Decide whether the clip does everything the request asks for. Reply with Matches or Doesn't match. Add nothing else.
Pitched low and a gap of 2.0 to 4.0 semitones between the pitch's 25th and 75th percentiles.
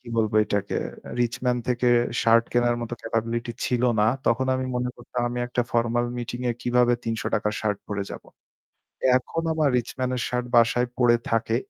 Doesn't match